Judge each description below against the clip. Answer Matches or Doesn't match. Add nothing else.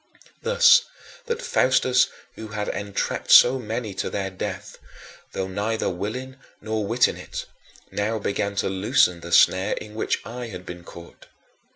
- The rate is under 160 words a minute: Matches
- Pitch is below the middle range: Matches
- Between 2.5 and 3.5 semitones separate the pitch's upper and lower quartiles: Doesn't match